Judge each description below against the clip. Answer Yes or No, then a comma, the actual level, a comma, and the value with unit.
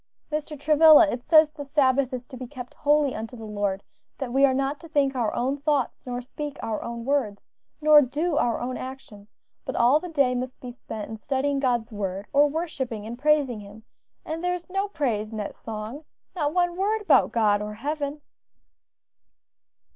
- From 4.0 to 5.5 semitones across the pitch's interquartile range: Yes, average, 4.3 semitones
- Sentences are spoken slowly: No, average, 190 wpm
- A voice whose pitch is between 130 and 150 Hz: No, very high, 265 Hz